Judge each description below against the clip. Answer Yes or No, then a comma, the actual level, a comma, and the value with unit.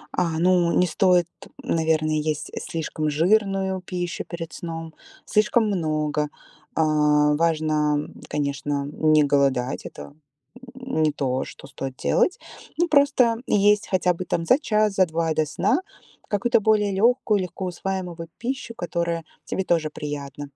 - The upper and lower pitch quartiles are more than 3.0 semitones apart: Yes, average, 4.2 semitones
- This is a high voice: No, medium, 165 Hz